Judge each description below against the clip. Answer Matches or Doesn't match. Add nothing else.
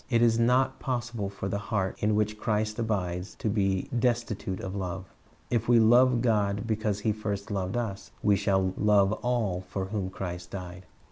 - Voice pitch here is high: Doesn't match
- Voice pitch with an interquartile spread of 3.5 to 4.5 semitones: Doesn't match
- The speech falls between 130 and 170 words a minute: Doesn't match